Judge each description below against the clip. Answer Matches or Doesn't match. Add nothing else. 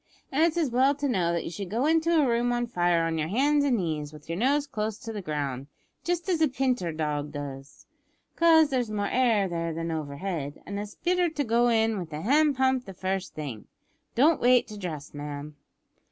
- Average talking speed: Doesn't match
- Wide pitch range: Matches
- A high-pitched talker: Matches